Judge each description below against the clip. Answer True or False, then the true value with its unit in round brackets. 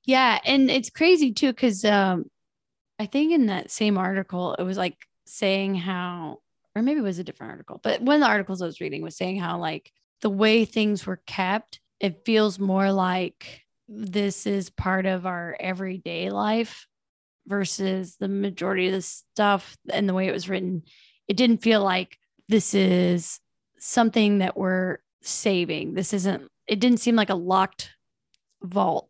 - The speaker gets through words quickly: False (175 wpm)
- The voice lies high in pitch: True (195 Hz)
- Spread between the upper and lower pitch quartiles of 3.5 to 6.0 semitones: False (2.8 semitones)